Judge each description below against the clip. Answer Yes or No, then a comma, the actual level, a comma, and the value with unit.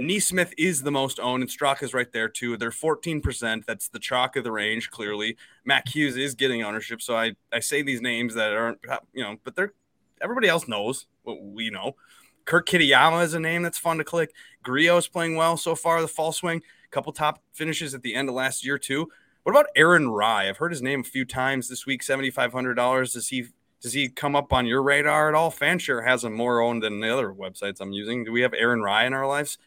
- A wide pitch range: No, average, 4.6 semitones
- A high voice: No, low, 135 Hz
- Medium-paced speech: No, fast, 235 wpm